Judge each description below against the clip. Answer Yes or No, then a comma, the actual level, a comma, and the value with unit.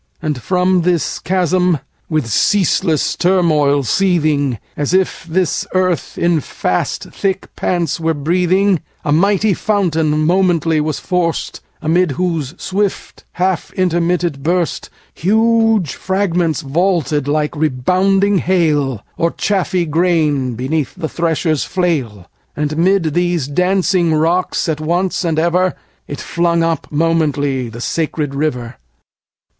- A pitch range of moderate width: Yes, average, 3.4 semitones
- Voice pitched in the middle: Yes, medium, 170 Hz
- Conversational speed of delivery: No, slow, 105 wpm